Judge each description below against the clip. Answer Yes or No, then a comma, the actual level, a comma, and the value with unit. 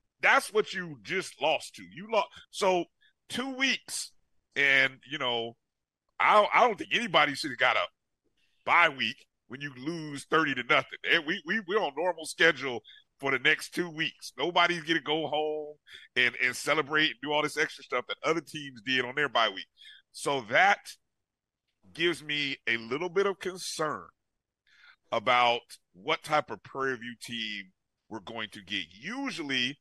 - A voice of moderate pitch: Yes, medium, 150 Hz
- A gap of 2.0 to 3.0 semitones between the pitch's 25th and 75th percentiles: No, average, 5.1 semitones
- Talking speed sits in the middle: Yes, average, 175 wpm